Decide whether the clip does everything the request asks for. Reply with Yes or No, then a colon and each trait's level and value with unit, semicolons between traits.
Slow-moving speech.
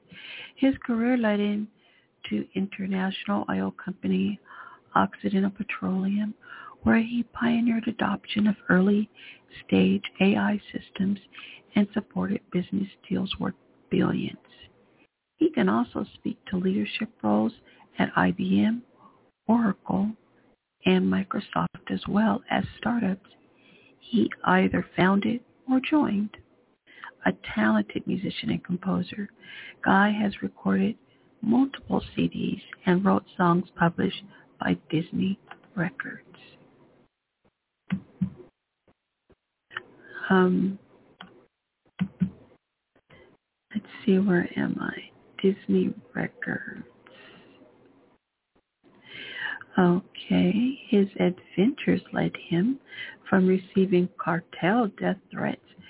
Yes: slow, 85 wpm